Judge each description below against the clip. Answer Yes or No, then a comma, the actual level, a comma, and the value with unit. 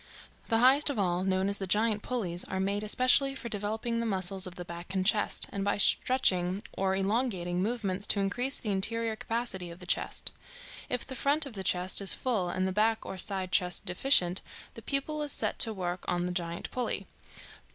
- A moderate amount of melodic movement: Yes, average, 3.9 semitones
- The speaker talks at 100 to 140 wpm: No, fast, 205 wpm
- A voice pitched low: No, high, 200 Hz